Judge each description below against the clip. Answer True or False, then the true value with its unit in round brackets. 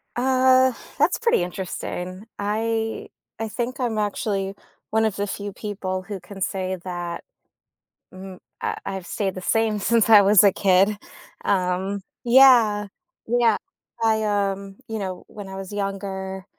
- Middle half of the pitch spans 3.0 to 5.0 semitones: False (2.6 semitones)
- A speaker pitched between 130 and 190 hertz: False (205 Hz)